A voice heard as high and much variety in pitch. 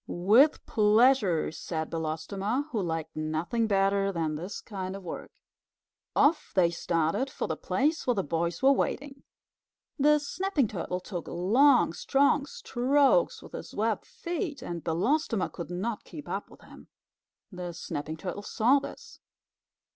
Yes: high, 205 Hz; wide, 8.1 semitones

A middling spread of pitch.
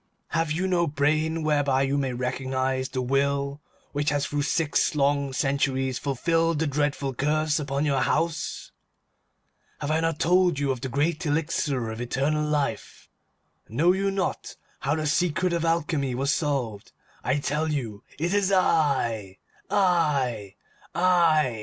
Yes: average, 3.3 semitones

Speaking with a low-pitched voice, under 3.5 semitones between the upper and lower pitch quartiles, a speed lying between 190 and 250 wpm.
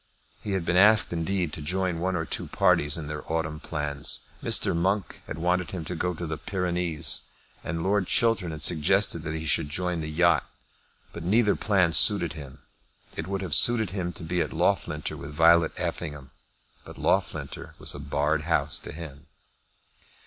No: very low, 85 Hz; average, 3.1 semitones; average, 180 wpm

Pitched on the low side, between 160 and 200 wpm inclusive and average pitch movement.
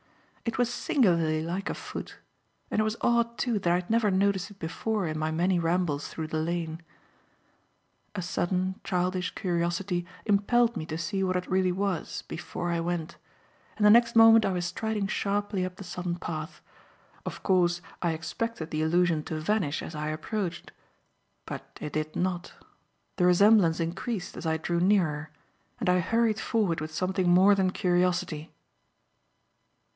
No: medium, 180 Hz; average, 165 wpm; average, 3.3 semitones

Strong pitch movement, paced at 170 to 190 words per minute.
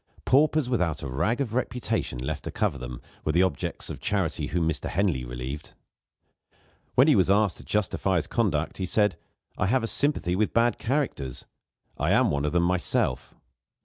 Yes: wide, 7.8 semitones; average, 180 wpm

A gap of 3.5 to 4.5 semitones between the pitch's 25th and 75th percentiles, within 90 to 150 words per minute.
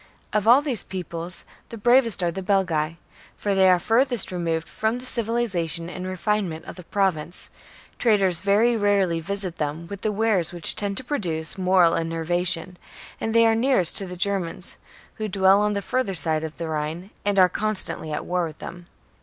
No: average, 3.9 semitones; average, 185 wpm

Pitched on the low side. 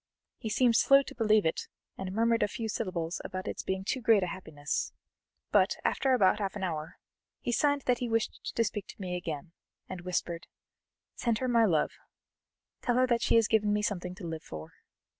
No: high, 205 Hz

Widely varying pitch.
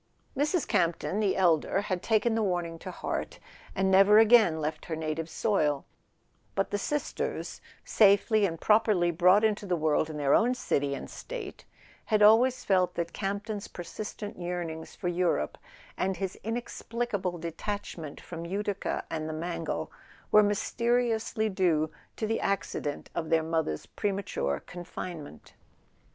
No: average, 4.5 semitones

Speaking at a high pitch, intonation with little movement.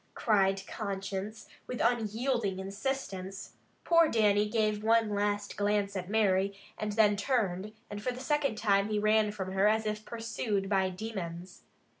Yes: high, 210 Hz; narrow, 2.1 semitones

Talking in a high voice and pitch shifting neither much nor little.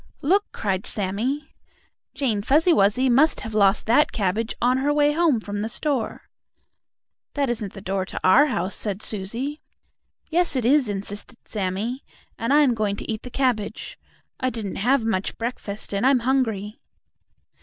Yes: high, 230 Hz; average, 5.0 semitones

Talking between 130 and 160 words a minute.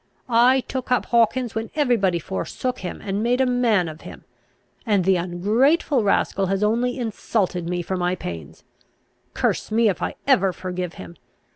No: average, 170 wpm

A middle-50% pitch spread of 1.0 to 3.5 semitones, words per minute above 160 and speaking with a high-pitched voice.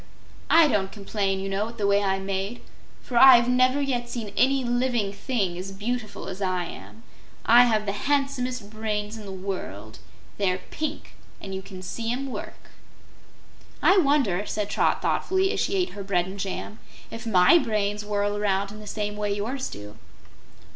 No: average, 4.0 semitones; average, 180 wpm; high, 210 Hz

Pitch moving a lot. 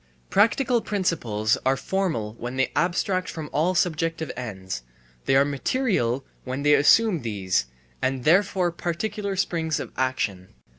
Yes: wide, 6.9 semitones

